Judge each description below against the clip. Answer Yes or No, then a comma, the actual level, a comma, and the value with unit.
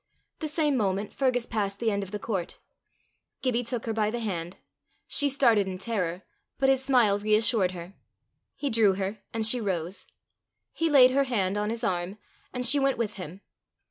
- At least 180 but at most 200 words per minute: Yes, average, 185 wpm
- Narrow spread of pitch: No, average, 4.4 semitones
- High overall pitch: Yes, high, 220 Hz